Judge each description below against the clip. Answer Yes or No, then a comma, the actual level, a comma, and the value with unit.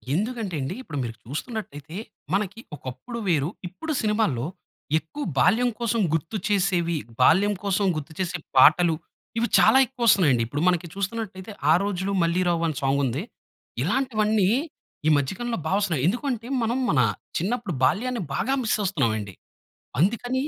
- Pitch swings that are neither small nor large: No, wide, 6.3 semitones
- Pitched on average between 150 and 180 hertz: No, high, 190 Hz